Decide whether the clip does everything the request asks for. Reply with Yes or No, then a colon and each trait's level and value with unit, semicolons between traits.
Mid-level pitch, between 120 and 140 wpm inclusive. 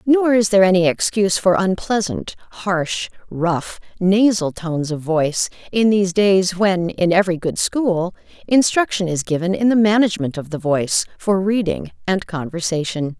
No: medium, 180 Hz; average, 155 wpm